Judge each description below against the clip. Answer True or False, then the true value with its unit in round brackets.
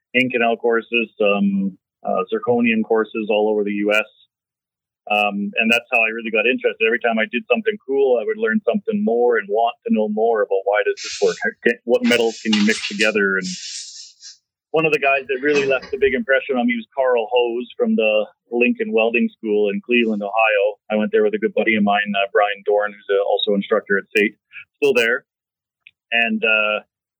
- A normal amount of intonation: False (6.2 semitones)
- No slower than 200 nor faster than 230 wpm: True (205 wpm)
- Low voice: True (115 Hz)